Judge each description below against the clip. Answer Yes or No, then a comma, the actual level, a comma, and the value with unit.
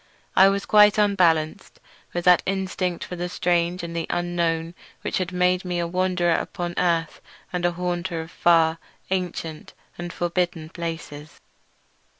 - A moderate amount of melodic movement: No, narrow, 1.4 semitones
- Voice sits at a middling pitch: Yes, medium, 175 Hz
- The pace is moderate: Yes, average, 150 wpm